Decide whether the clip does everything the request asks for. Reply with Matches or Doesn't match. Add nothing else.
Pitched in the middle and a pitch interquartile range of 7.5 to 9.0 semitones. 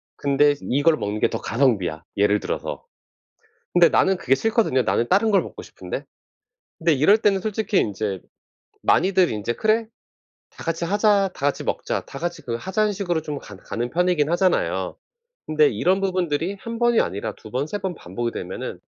Matches